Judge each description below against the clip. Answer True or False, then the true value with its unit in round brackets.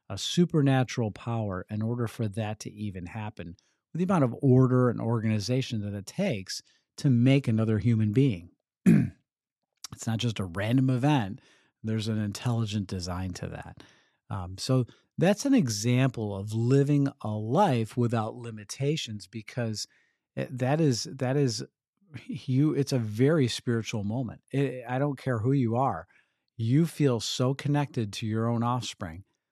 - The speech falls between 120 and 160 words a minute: True (150 wpm)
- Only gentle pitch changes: False (3.9 semitones)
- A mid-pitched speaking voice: False (120 Hz)